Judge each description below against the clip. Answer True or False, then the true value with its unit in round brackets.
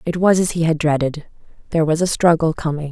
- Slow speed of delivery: False (205 wpm)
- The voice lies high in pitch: False (160 Hz)